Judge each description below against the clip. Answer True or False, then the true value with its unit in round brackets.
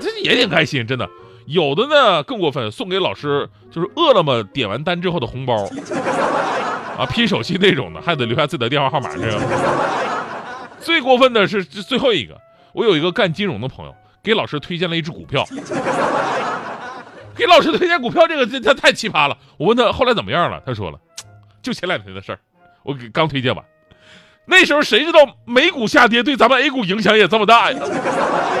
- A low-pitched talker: False (180 Hz)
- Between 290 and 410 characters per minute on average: True (300 characters per minute)